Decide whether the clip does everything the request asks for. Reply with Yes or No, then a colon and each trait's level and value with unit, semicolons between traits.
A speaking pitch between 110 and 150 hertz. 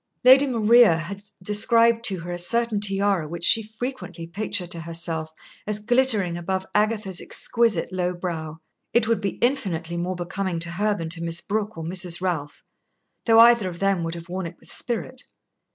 No: high, 190 Hz